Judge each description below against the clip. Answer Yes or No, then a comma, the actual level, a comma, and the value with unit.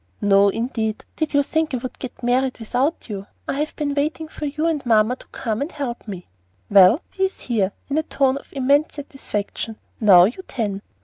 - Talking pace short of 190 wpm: No, average, 200 wpm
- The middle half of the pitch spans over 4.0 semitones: Yes, average, 5.1 semitones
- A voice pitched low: No, very high, 255 Hz